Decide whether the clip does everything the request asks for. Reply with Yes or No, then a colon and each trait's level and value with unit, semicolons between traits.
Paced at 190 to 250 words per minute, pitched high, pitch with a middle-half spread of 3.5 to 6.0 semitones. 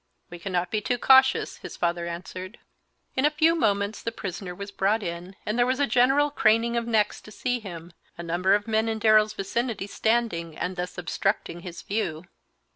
Yes: average, 195 wpm; high, 210 Hz; average, 4.7 semitones